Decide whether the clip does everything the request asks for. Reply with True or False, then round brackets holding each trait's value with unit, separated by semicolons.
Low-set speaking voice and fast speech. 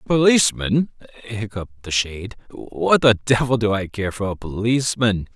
False (110 Hz; 145 wpm)